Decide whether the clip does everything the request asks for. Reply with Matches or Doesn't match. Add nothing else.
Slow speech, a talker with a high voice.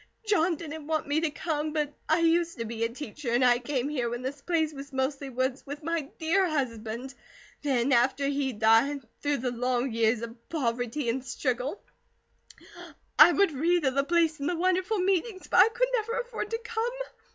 Doesn't match